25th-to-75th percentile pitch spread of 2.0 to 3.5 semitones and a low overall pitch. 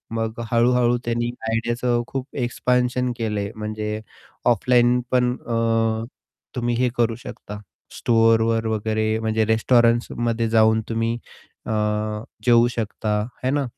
No: narrow, 1.6 semitones; low, 115 Hz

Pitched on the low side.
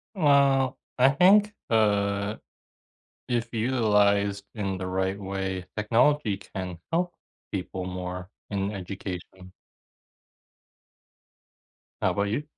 Yes: low, 100 Hz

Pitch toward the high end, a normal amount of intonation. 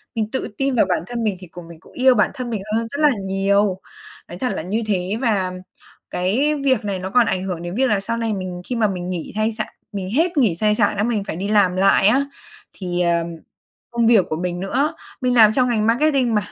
Yes: high, 210 Hz; average, 4.5 semitones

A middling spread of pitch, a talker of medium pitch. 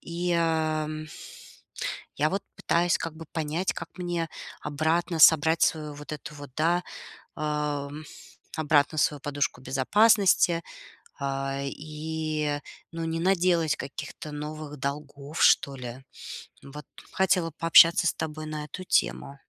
No: narrow, 2.2 semitones; medium, 155 Hz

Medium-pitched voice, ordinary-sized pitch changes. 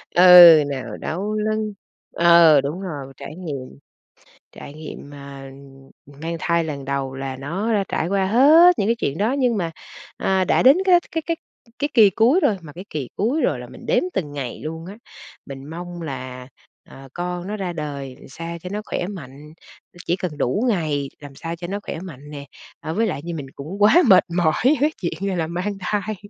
No: medium, 170 Hz; wide, 6.0 semitones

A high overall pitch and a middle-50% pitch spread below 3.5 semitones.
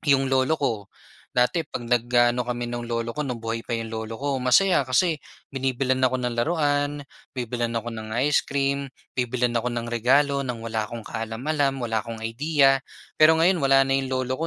No: low, 130 Hz; average, 2.9 semitones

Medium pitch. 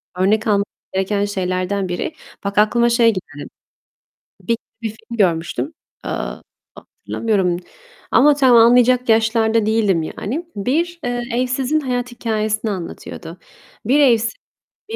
No: high, 220 Hz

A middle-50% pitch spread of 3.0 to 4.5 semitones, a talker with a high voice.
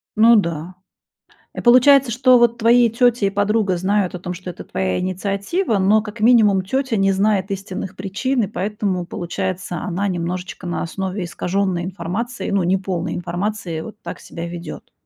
Yes: average, 3.4 semitones; high, 195 Hz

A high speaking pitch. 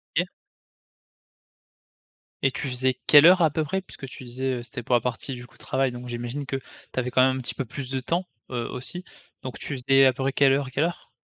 No: low, 130 Hz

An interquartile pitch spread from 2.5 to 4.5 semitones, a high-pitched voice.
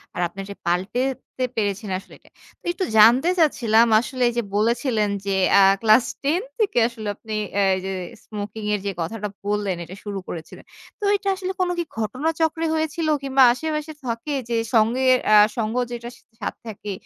No: average, 5.3 semitones; high, 230 Hz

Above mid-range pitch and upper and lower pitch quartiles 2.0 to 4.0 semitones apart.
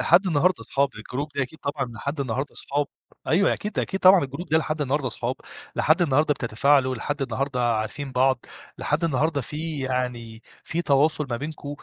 No: medium, 140 Hz; average, 3.3 semitones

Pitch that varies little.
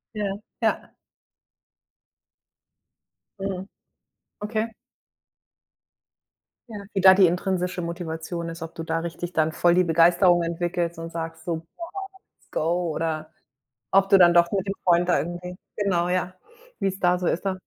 Yes: narrow, 2.1 semitones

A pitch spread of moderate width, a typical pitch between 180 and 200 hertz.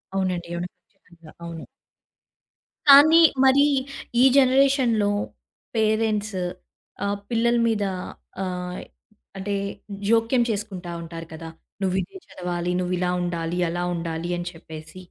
Yes: average, 4.6 semitones; medium, 185 Hz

